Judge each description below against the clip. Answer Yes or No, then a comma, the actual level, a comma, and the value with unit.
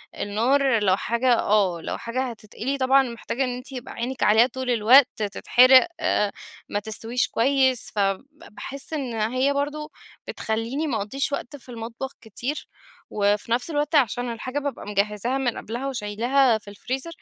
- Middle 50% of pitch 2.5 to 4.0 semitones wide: Yes, average, 3.7 semitones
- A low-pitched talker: No, high, 245 Hz